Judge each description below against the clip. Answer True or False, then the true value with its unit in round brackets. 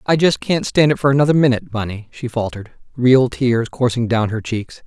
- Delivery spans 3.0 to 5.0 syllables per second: False (5.6 syllables/s)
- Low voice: True (125 Hz)